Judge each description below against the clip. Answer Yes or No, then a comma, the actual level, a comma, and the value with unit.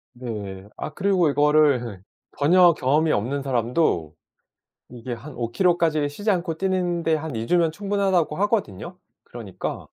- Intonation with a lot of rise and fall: Yes, wide, 6.5 semitones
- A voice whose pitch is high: No, medium, 150 Hz